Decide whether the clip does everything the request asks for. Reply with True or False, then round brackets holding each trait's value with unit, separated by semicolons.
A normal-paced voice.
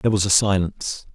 False (210 wpm)